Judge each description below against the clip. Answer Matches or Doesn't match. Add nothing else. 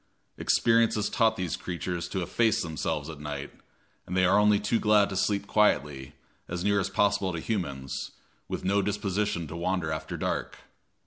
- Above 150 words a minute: Matches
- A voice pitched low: Matches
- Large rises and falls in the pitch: Doesn't match